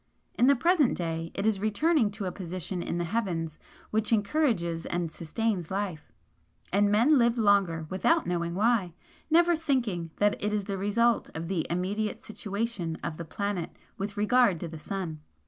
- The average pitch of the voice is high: Yes, high, 200 Hz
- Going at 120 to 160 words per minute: No, average, 170 wpm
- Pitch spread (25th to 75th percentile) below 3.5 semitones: No, average, 4.7 semitones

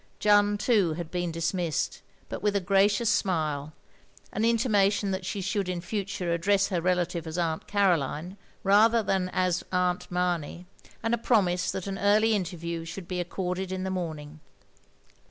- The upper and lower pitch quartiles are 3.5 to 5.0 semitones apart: No, average, 2.7 semitones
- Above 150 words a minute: Yes, average, 170 wpm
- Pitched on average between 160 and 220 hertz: Yes, medium, 185 Hz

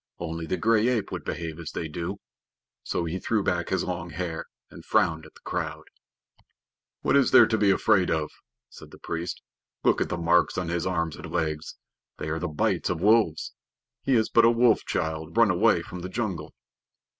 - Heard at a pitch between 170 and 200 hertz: No, very low, 85 Hz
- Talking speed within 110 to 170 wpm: No, average, 200 wpm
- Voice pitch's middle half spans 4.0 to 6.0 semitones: Yes, average, 4.3 semitones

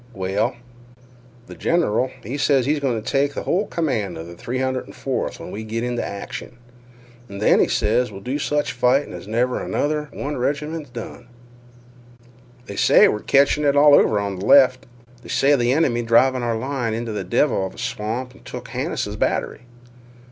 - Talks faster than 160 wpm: Yes, average, 180 wpm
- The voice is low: Yes, low, 125 Hz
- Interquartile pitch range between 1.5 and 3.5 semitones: No, average, 4.4 semitones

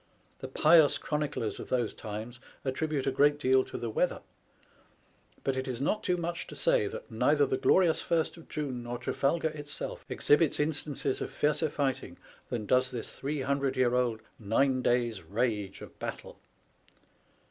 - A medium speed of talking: Yes, average, 165 wpm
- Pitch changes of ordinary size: Yes, average, 3.9 semitones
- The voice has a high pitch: No, low, 135 Hz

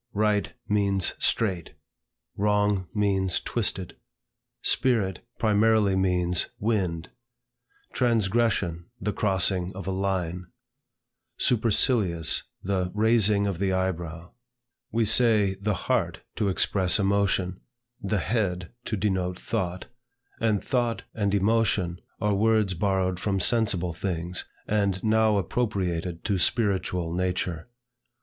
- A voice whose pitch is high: No, low, 100 Hz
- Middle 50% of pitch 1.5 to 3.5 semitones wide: Yes, average, 2.8 semitones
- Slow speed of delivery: Yes, slow, 105 wpm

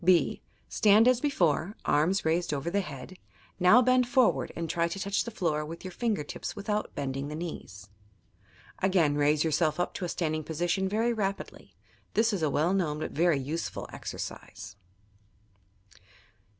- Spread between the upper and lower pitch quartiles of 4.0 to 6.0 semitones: Yes, average, 4.7 semitones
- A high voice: No, medium, 175 Hz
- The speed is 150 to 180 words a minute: Yes, average, 160 wpm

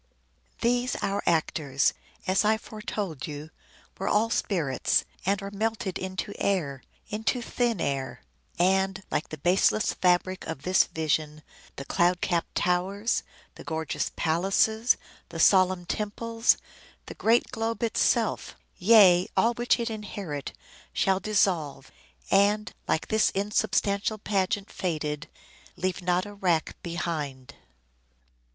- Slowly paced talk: Yes, slow, 120 wpm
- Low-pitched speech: No, high, 190 Hz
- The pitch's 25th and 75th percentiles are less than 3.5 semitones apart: No, average, 4.4 semitones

